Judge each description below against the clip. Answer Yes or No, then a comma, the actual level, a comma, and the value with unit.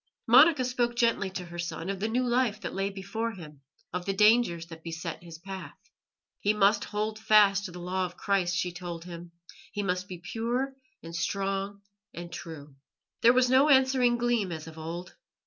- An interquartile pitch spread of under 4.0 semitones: No, average, 4.8 semitones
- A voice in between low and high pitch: No, high, 195 Hz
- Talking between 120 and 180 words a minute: No, average, 190 wpm